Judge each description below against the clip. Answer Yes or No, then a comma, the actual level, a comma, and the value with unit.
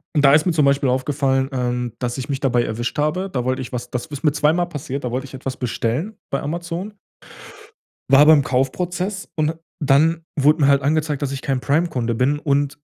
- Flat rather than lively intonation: No, average, 3.1 semitones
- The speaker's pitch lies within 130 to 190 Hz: Yes, medium, 140 Hz